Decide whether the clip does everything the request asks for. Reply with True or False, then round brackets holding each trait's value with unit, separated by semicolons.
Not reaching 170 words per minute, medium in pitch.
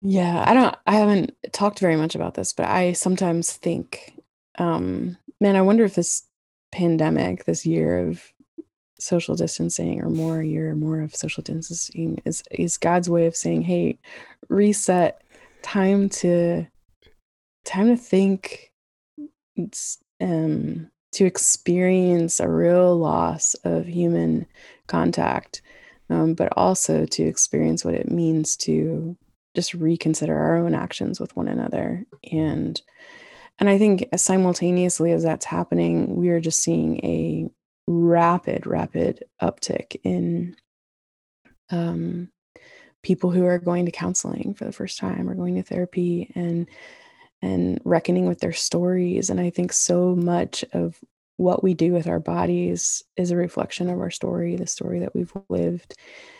True (145 wpm; 170 Hz)